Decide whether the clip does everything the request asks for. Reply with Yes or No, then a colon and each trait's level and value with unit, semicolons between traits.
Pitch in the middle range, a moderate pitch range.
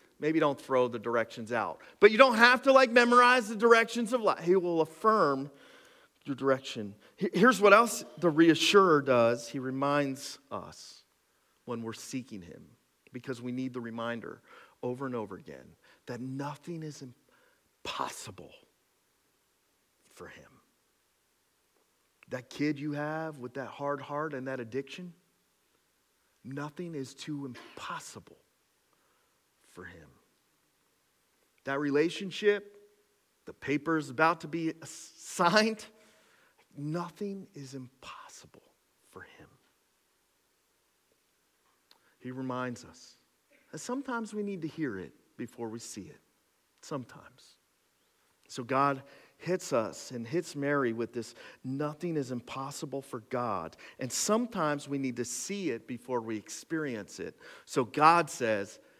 No: medium, 145 Hz; wide, 7.0 semitones